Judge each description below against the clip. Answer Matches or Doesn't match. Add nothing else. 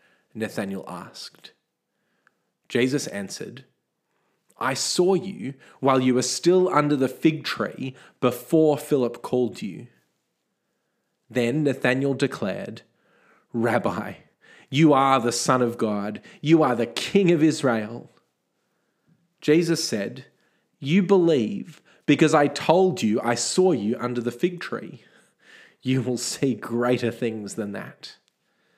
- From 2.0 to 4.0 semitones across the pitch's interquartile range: Doesn't match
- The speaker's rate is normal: Doesn't match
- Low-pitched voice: Matches